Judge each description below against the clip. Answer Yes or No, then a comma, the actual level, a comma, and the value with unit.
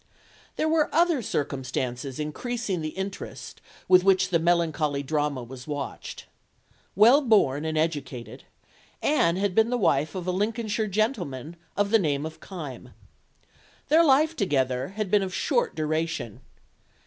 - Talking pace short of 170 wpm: Yes, average, 140 wpm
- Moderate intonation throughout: No, wide, 6.8 semitones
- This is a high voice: No, medium, 175 Hz